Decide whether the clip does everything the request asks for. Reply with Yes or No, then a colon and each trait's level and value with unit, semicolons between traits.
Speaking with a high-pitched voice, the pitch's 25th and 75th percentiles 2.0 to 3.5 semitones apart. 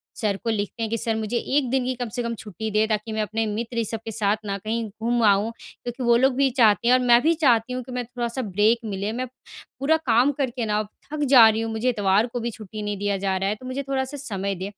Yes: high, 230 Hz; average, 2.9 semitones